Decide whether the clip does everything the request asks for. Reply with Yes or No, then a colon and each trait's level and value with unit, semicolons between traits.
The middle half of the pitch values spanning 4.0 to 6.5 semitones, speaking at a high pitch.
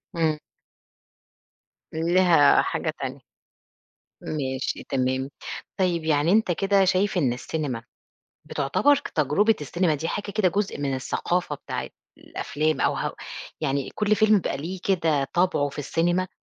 No: average, 4.6 semitones; medium, 165 Hz